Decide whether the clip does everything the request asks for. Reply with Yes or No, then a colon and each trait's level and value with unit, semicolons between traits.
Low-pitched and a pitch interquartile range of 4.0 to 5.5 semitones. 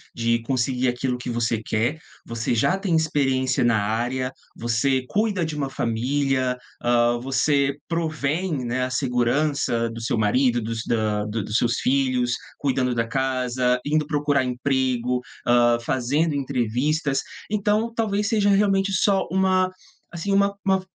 Yes: low, 130 Hz; average, 4.6 semitones